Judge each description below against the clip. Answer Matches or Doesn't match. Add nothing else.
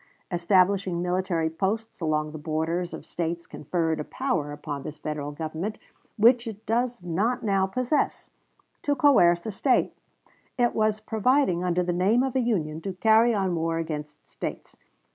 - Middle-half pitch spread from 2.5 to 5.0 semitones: Doesn't match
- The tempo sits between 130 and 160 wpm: Matches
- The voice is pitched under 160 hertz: Doesn't match